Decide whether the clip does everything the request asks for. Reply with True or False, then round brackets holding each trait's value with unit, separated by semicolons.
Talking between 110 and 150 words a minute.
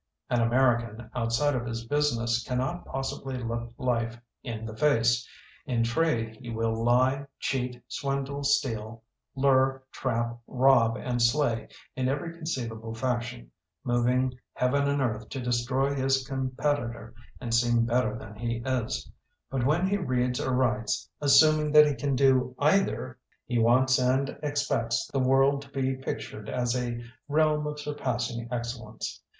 True (145 wpm)